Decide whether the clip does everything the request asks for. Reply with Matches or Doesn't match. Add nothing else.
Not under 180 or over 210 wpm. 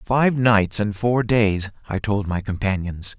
Doesn't match